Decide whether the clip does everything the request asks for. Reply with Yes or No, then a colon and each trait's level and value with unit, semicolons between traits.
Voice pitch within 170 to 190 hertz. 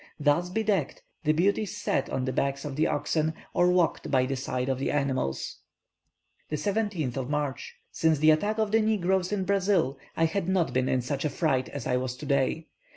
No: medium, 155 Hz